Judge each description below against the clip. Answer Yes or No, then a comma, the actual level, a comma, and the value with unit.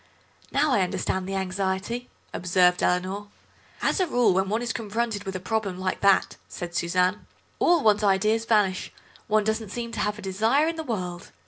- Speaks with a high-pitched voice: Yes, high, 205 Hz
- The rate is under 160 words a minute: No, average, 185 wpm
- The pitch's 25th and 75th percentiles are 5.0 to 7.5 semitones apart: No, average, 3.4 semitones